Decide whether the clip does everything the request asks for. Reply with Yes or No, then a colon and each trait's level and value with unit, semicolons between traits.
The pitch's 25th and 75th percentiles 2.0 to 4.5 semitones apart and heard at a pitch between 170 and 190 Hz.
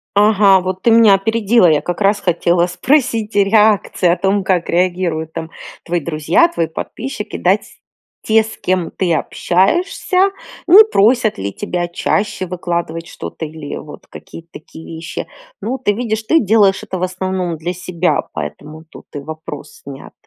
Yes: average, 4.2 semitones; medium, 185 Hz